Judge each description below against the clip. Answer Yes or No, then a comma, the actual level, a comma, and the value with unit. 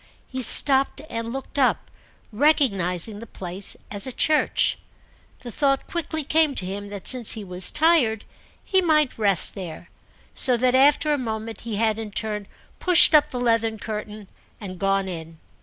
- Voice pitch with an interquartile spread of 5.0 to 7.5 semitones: Yes, average, 5.3 semitones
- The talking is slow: No, average, 165 wpm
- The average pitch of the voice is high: Yes, high, 225 Hz